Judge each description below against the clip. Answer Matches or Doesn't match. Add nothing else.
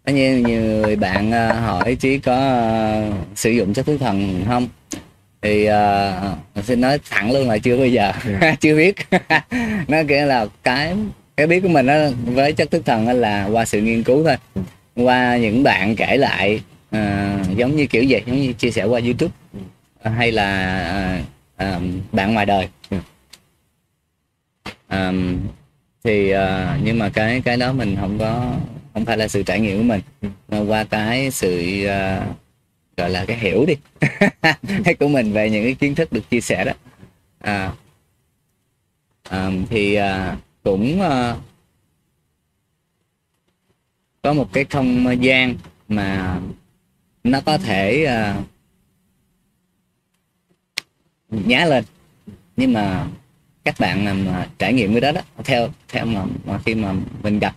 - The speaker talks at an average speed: Doesn't match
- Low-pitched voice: Matches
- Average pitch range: Matches